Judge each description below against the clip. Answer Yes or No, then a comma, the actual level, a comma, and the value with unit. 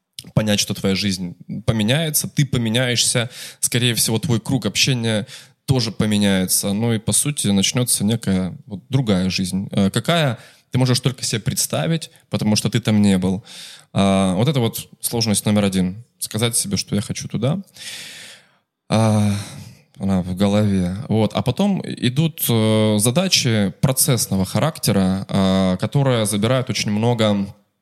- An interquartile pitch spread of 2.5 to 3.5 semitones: No, average, 4.6 semitones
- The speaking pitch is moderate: No, low, 115 Hz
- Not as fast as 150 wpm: Yes, average, 140 wpm